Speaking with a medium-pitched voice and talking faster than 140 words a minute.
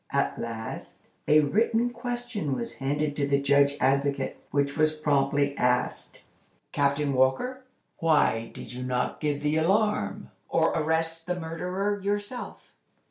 No: medium, 150 Hz; slow, 135 wpm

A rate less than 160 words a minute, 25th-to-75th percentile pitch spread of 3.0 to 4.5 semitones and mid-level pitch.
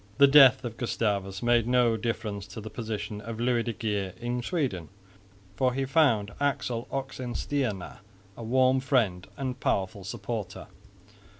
No: average, 140 wpm; average, 3.6 semitones; low, 115 Hz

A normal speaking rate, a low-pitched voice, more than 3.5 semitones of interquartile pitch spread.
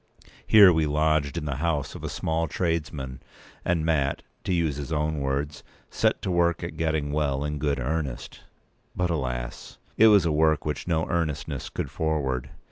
No: average, 180 wpm; very low, 75 Hz; average, 2.7 semitones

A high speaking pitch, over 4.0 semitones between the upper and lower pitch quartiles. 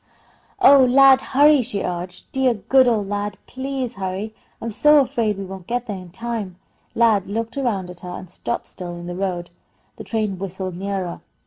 Yes: high, 205 Hz; average, 4.8 semitones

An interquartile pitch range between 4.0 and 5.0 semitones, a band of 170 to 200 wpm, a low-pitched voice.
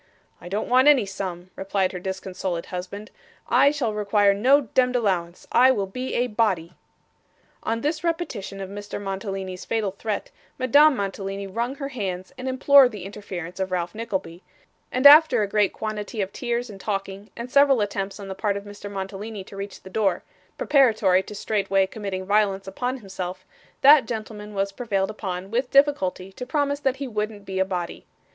No: average, 4.3 semitones; average, 180 wpm; high, 205 Hz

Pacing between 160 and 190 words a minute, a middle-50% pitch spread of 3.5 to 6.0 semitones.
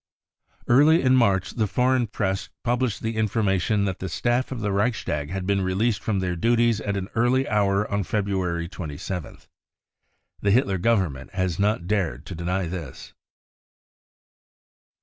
No: average, 150 wpm; average, 3.9 semitones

